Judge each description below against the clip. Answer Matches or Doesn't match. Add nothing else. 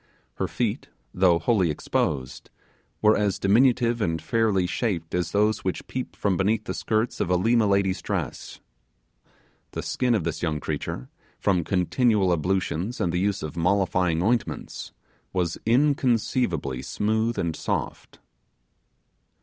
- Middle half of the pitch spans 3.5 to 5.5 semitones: Matches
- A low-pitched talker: Matches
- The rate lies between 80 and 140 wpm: Matches